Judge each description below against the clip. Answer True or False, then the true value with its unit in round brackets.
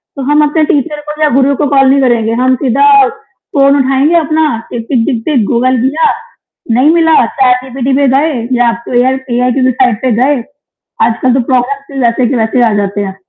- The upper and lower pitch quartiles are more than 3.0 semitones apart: False (2.4 semitones)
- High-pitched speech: True (265 Hz)